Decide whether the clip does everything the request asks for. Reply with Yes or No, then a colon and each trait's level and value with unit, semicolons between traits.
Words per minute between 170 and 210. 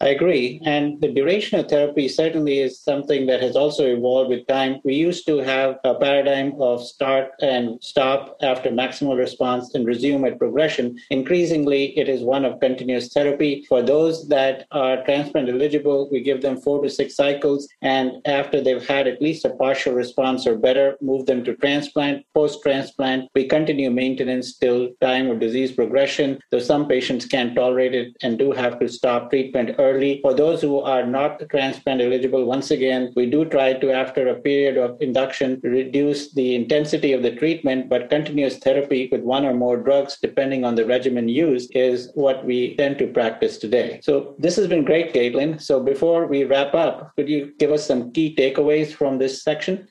Yes: average, 185 wpm